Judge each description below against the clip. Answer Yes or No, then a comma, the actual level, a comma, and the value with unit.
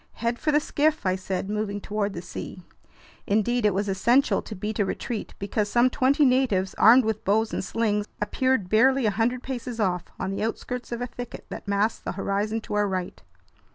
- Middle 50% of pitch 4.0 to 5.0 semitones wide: No, average, 3.5 semitones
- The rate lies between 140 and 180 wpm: No, average, 200 wpm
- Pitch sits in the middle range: No, high, 215 Hz